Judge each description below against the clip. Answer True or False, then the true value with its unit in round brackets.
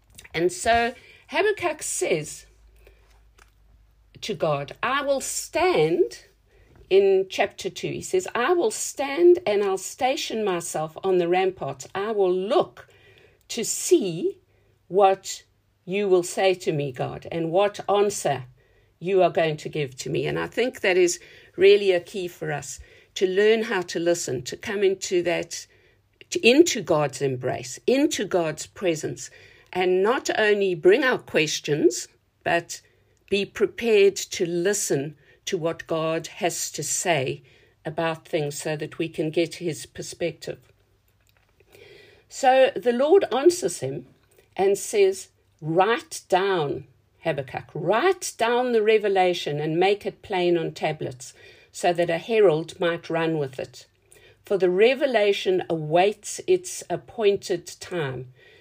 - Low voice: False (195 Hz)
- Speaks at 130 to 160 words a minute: True (135 wpm)